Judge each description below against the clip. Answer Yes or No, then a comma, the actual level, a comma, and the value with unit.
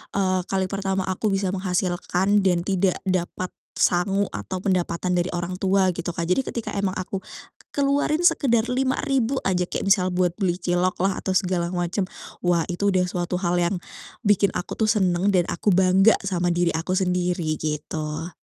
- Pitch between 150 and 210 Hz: Yes, medium, 185 Hz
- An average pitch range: No, narrow, 2.0 semitones